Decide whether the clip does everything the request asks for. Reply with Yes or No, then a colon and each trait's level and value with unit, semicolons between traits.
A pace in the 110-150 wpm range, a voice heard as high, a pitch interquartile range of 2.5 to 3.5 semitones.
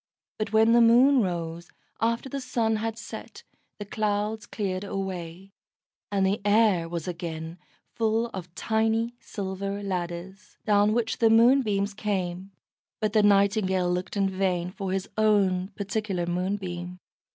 Yes: average, 140 wpm; high, 200 Hz; average, 3.1 semitones